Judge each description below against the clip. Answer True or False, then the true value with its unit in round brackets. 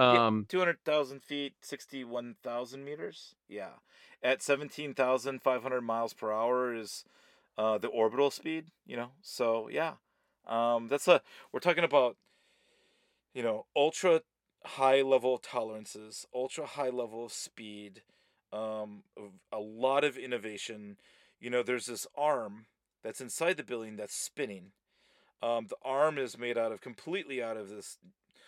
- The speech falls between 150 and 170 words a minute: False (135 wpm)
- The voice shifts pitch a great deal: False (4.2 semitones)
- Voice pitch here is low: True (125 Hz)